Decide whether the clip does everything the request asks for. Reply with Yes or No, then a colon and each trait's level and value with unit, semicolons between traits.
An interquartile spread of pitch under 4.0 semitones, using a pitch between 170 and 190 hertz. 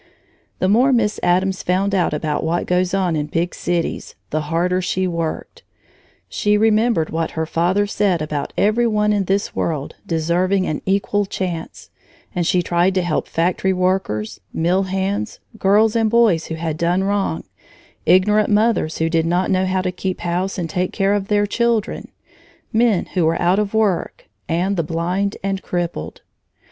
Yes: average, 3.2 semitones; medium, 185 Hz